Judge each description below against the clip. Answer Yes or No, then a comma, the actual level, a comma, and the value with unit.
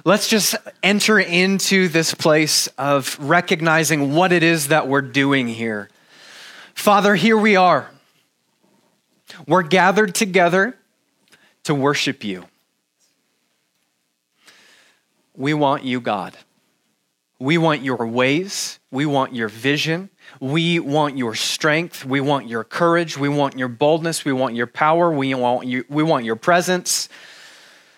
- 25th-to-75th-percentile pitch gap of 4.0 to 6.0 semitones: Yes, average, 4.9 semitones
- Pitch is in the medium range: Yes, medium, 155 Hz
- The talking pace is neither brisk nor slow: No, slow, 130 wpm